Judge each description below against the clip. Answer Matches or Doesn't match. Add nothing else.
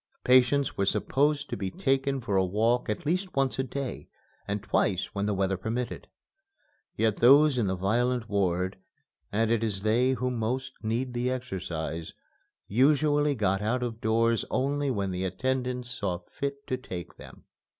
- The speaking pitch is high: Doesn't match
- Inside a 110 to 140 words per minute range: Doesn't match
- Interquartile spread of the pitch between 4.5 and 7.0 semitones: Matches